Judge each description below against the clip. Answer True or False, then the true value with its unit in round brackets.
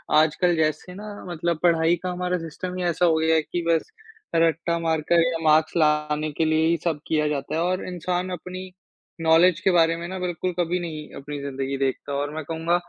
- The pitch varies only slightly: True (2.3 semitones)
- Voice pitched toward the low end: False (165 Hz)